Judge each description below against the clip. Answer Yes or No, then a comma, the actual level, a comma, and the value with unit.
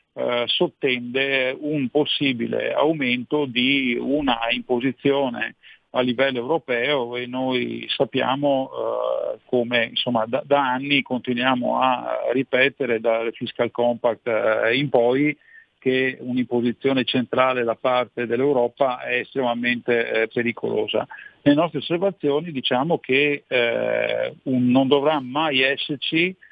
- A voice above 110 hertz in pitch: Yes, low, 130 Hz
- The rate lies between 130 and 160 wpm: No, slow, 115 wpm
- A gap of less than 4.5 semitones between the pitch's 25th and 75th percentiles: Yes, average, 2.7 semitones